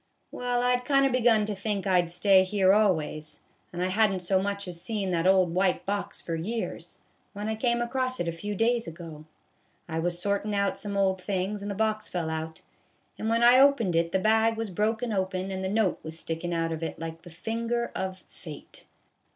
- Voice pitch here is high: Yes, high, 195 Hz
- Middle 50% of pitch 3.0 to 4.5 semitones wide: Yes, average, 4.1 semitones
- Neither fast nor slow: No, fast, 220 wpm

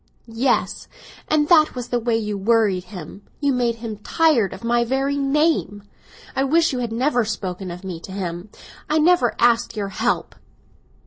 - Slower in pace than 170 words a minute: No, average, 175 wpm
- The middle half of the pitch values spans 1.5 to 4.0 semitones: No, average, 5.2 semitones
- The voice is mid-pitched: No, high, 235 Hz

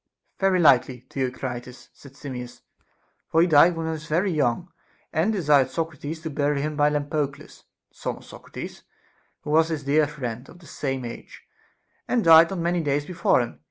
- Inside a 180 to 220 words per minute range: Yes, average, 185 wpm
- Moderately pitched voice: Yes, medium, 150 Hz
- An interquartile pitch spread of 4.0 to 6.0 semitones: No, average, 3.3 semitones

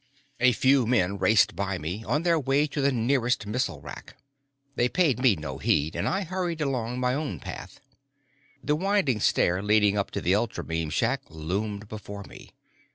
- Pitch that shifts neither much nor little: No, wide, 6.1 semitones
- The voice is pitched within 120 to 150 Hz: No, low, 110 Hz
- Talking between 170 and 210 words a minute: Yes, average, 175 wpm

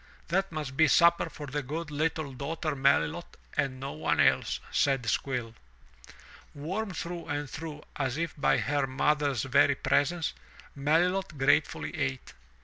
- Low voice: No, medium, 145 Hz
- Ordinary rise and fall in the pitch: Yes, average, 3.0 semitones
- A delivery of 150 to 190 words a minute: No, average, 140 wpm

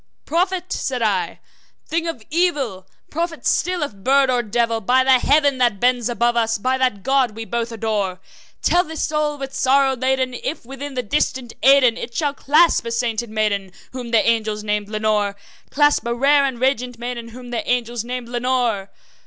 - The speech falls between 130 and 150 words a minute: No, average, 180 wpm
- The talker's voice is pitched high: Yes, high, 245 Hz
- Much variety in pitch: No, average, 3.5 semitones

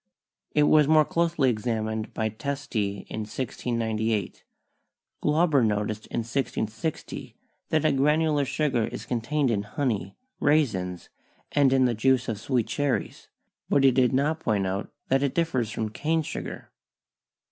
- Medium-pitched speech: No, low, 130 Hz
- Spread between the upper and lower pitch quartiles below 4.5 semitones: No, average, 5.0 semitones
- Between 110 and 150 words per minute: Yes, average, 140 wpm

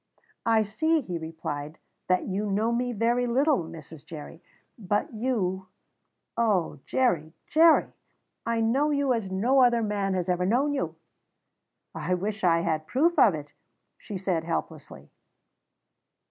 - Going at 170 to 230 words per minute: No, average, 140 wpm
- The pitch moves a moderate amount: No, wide, 6.2 semitones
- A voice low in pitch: No, high, 205 Hz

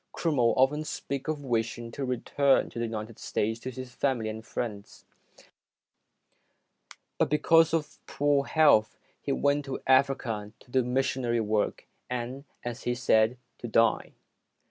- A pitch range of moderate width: Yes, average, 3.4 semitones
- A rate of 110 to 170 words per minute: Yes, average, 145 wpm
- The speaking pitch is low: Yes, low, 125 Hz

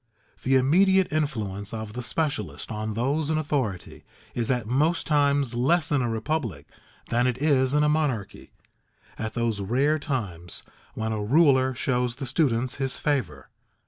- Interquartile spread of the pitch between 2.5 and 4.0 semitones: No, average, 4.7 semitones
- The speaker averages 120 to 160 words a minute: Yes, average, 155 wpm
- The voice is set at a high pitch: No, low, 130 Hz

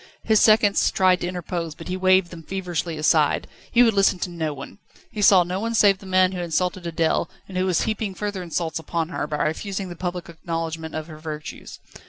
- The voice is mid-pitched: Yes, medium, 180 Hz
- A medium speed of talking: No, fast, 220 wpm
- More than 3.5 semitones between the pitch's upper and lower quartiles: No, average, 2.7 semitones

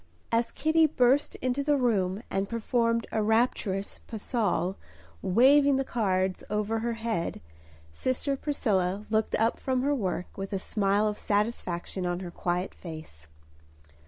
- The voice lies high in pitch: Yes, high, 220 Hz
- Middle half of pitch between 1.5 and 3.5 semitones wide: No, average, 4.6 semitones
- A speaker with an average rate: Yes, average, 145 wpm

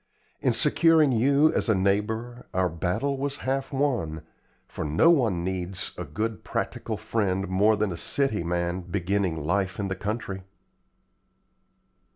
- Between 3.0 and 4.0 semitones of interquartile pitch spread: No, average, 5.2 semitones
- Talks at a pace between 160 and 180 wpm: No, average, 145 wpm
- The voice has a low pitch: Yes, low, 100 Hz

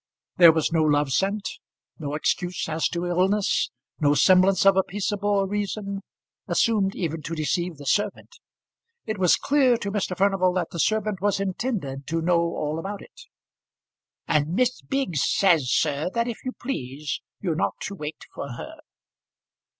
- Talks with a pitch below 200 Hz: Yes, medium, 185 Hz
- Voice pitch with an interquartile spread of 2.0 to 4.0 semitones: No, average, 4.4 semitones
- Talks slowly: No, average, 160 wpm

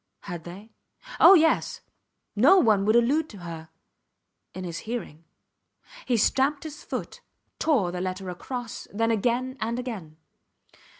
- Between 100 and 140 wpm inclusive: Yes, slow, 135 wpm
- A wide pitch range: Yes, wide, 5.9 semitones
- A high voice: Yes, high, 225 Hz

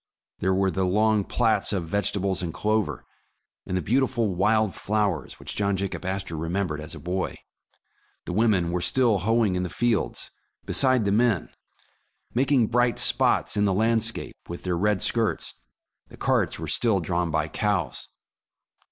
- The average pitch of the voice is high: No, low, 100 Hz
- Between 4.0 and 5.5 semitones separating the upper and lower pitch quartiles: No, average, 3.6 semitones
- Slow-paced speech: No, average, 160 wpm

